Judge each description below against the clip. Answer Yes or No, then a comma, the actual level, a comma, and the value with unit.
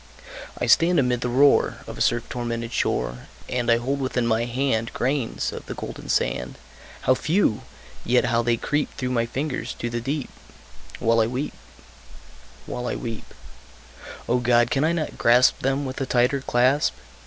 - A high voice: No, low, 125 Hz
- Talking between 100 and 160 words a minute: No, average, 175 wpm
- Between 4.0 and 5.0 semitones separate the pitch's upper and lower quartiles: No, narrow, 2.5 semitones